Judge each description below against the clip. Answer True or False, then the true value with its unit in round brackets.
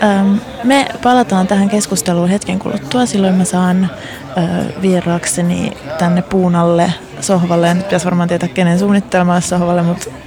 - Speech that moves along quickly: False (125 wpm)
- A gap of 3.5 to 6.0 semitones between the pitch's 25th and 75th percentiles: False (2.5 semitones)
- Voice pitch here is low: False (180 Hz)